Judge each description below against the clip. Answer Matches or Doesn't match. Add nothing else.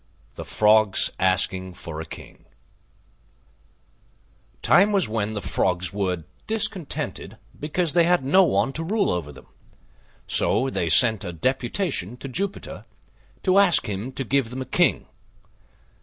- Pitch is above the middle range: Doesn't match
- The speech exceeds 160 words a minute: Doesn't match